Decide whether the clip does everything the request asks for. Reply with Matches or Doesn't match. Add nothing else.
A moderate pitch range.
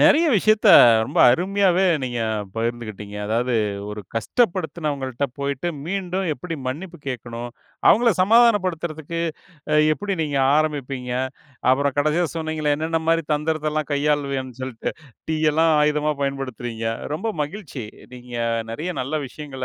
Matches